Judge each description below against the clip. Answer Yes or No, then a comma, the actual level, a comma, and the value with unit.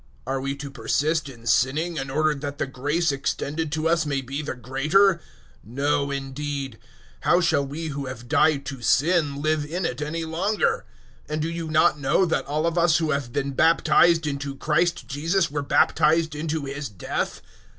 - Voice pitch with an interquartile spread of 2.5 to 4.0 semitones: Yes, average, 2.8 semitones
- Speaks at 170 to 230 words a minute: Yes, average, 190 wpm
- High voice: No, medium, 150 Hz